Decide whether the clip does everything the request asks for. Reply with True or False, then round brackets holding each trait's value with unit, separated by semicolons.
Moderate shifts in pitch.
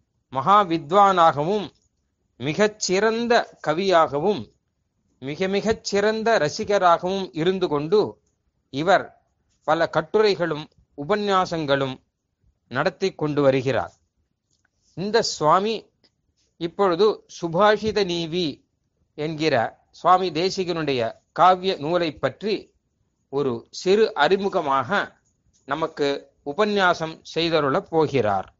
False (6.2 semitones)